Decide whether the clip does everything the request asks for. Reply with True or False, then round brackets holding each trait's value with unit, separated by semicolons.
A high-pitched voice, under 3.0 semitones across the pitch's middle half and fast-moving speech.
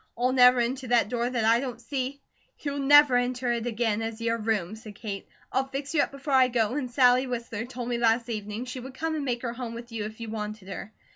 True (240 Hz; 2.4 semitones; 255 wpm)